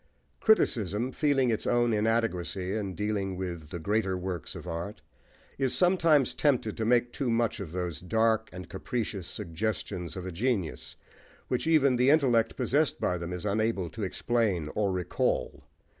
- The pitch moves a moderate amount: Yes, average, 4.8 semitones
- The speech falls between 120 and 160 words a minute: Yes, average, 155 wpm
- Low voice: Yes, low, 105 Hz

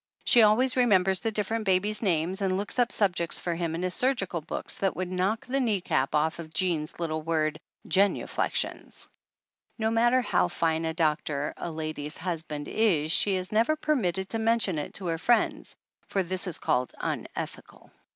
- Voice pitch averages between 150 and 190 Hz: Yes, medium, 185 Hz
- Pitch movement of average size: Yes, average, 5.0 semitones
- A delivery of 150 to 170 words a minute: No, average, 180 wpm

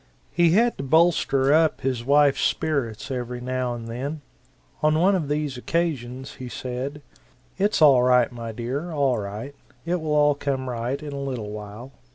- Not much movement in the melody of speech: No, average, 3.6 semitones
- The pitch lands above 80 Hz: Yes, low, 135 Hz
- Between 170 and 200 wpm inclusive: Yes, average, 175 wpm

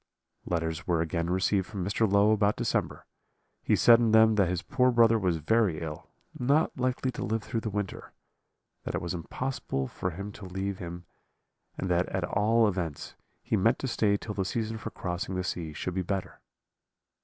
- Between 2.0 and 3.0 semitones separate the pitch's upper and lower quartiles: No, average, 4.1 semitones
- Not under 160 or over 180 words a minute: No, average, 190 wpm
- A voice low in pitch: Yes, low, 100 Hz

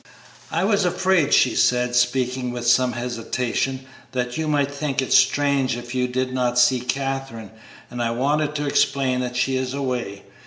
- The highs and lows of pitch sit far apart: No, narrow, 2.4 semitones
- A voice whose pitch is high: No, low, 130 Hz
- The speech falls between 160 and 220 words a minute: Yes, average, 170 wpm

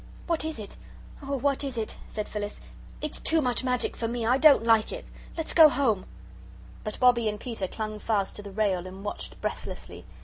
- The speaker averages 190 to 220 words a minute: Yes, average, 200 wpm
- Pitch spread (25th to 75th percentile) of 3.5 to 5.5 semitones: Yes, average, 4.7 semitones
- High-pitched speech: Yes, high, 230 Hz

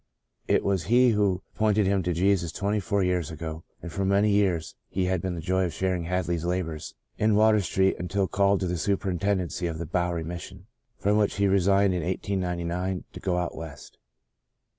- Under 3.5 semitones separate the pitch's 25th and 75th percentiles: Yes, narrow, 2.4 semitones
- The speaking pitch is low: Yes, very low, 95 Hz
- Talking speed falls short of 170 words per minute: No, average, 185 wpm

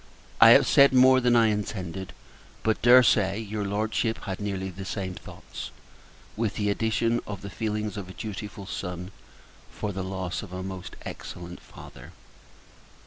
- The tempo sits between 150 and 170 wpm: Yes, average, 160 wpm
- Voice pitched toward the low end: Yes, low, 100 Hz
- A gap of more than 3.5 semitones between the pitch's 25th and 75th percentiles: No, average, 2.8 semitones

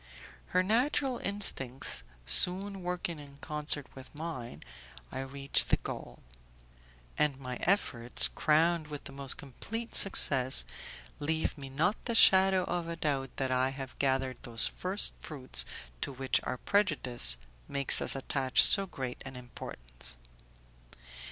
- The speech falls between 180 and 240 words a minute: No, slow, 135 wpm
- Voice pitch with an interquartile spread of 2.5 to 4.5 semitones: No, wide, 5.4 semitones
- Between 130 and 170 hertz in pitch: Yes, medium, 140 Hz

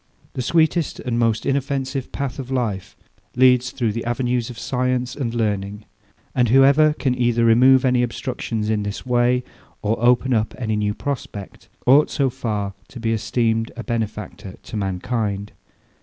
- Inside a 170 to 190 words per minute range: No, average, 155 wpm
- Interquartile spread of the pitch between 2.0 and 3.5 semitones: Yes, average, 2.9 semitones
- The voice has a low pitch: Yes, low, 120 Hz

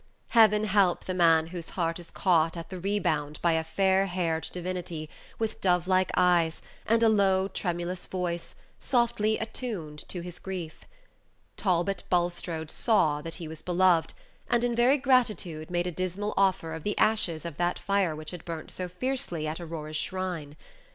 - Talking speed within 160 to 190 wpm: Yes, average, 170 wpm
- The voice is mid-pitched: Yes, medium, 180 Hz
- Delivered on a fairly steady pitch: No, average, 3.2 semitones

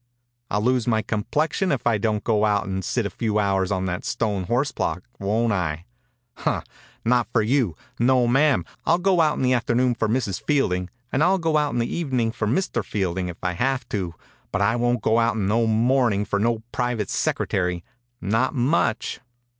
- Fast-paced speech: Yes, fast, 210 wpm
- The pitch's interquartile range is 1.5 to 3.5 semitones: No, average, 4.0 semitones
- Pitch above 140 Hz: No, low, 115 Hz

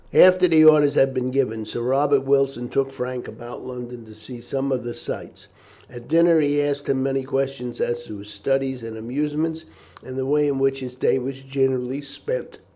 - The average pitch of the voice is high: No, low, 135 Hz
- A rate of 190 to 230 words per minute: Yes, average, 200 wpm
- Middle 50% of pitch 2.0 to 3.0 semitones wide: Yes, narrow, 2.4 semitones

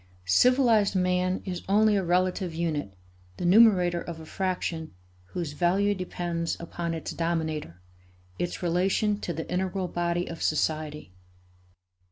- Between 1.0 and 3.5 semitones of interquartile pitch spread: Yes, narrow, 2.4 semitones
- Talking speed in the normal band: No, slow, 130 wpm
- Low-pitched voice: No, medium, 175 Hz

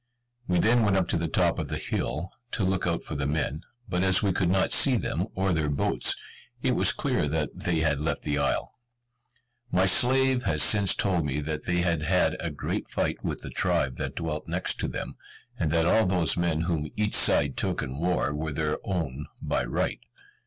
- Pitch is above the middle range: No, very low, 85 Hz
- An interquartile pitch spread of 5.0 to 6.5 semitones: No, average, 3.7 semitones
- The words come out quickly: Yes, fast, 210 wpm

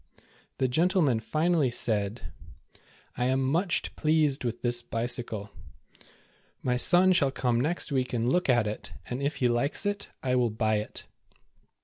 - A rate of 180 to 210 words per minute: No, average, 155 wpm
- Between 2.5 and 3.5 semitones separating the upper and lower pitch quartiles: No, average, 4.4 semitones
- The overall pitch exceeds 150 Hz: No, low, 125 Hz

